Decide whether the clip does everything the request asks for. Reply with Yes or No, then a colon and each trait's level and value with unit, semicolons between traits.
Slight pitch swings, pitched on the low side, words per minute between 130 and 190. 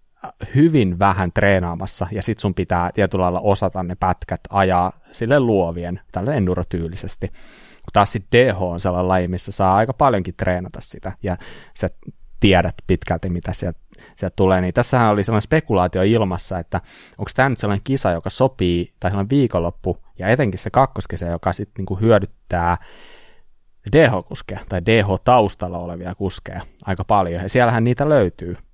No: average, 3.3 semitones; very low, 95 Hz; average, 150 wpm